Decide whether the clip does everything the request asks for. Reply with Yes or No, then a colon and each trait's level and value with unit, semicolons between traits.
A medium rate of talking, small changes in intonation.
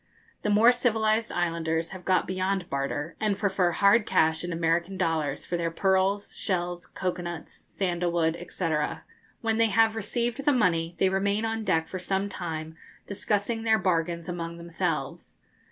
No: average, 160 wpm; average, 3.6 semitones